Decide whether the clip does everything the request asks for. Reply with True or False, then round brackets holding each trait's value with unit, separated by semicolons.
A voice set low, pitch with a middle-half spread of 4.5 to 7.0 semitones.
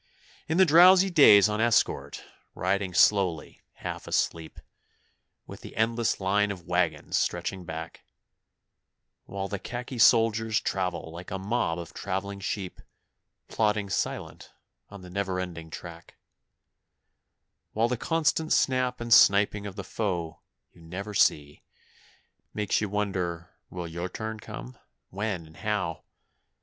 False (100 Hz; 3.8 semitones)